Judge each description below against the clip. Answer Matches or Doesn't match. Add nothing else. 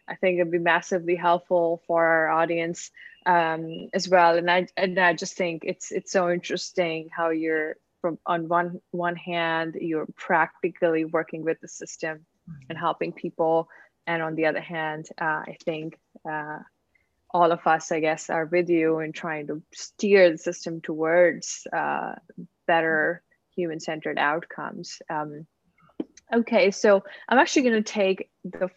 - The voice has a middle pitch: Matches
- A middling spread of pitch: Doesn't match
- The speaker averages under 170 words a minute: Matches